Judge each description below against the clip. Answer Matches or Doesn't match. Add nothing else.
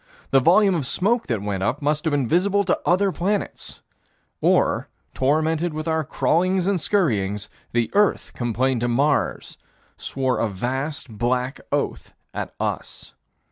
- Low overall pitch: Doesn't match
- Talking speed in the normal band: Matches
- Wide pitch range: Matches